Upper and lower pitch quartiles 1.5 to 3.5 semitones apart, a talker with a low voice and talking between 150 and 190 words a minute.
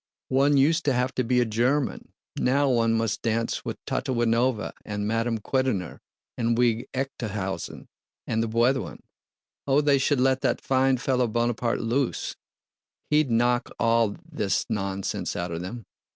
No: average, 2.8 semitones; low, 120 Hz; average, 140 wpm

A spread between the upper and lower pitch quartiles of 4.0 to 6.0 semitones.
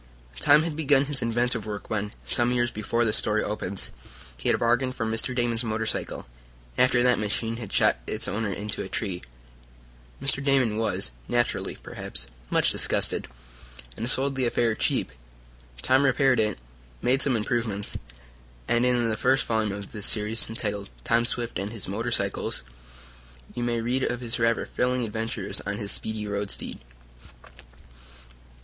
No: average, 2.7 semitones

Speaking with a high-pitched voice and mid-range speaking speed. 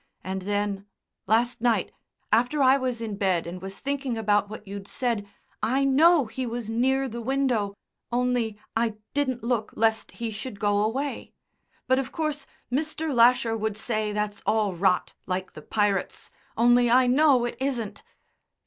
Yes: high, 230 Hz; average, 160 wpm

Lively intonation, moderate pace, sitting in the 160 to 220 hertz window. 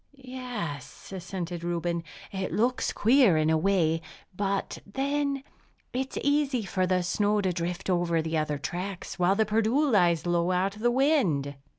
Yes: wide, 5.8 semitones; average, 160 wpm; high, 190 Hz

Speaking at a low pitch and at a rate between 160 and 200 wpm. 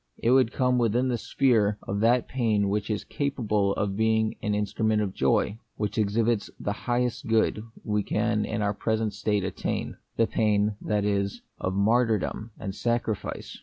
Yes: low, 110 Hz; average, 175 wpm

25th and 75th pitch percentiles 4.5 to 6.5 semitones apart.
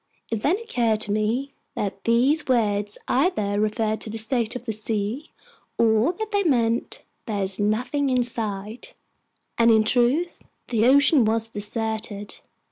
No: average, 3.3 semitones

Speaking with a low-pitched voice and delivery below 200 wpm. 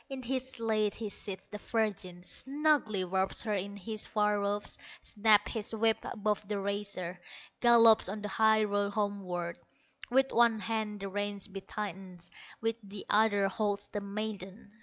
No: high, 210 Hz; average, 160 wpm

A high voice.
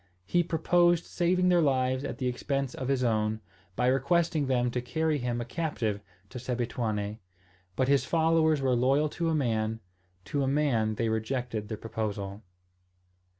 No: low, 130 Hz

